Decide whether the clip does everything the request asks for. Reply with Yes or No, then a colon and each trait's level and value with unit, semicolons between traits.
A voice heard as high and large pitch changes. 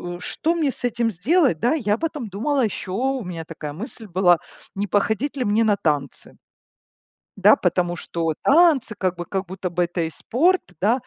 Yes: high, 205 Hz; wide, 7.0 semitones